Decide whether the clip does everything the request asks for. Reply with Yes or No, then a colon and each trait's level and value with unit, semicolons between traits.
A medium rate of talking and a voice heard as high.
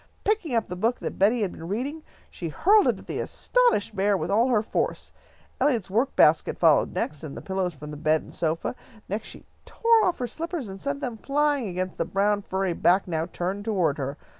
No: fast, 215 wpm; high, 200 Hz